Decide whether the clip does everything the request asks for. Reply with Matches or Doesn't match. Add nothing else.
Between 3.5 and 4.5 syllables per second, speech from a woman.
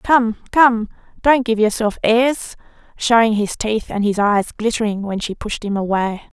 Matches